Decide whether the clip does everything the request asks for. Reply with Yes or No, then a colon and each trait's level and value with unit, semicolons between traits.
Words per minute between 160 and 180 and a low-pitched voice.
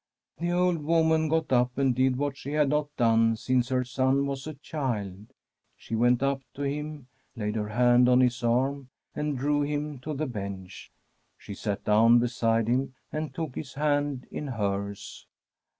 Yes: average, 175 wpm; low, 130 Hz